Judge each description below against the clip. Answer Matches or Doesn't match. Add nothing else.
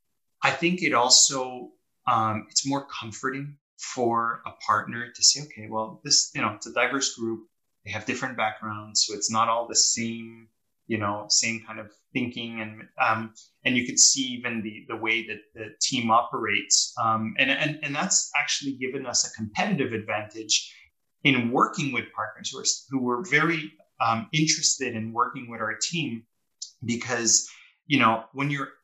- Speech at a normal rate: Matches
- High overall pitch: Doesn't match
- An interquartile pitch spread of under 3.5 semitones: Doesn't match